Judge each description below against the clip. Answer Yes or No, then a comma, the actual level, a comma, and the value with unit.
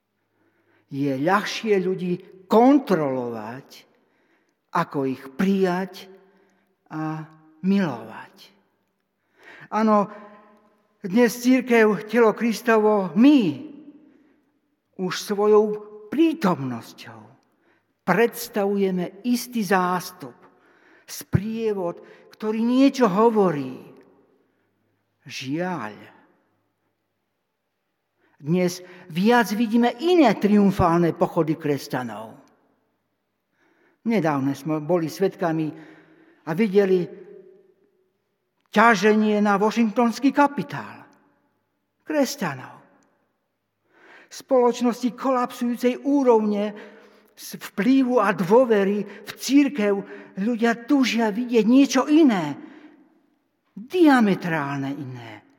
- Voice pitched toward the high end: Yes, high, 210 Hz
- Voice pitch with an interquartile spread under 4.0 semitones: No, wide, 5.5 semitones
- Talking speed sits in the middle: No, slow, 65 wpm